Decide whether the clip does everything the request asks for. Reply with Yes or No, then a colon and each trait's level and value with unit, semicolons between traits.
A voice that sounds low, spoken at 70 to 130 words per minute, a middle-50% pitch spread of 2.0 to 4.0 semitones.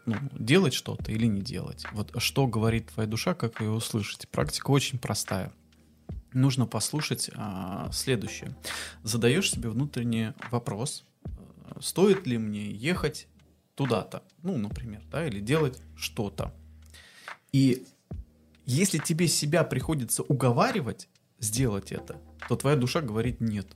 No: low, 115 Hz; average, 125 wpm; average, 5.0 semitones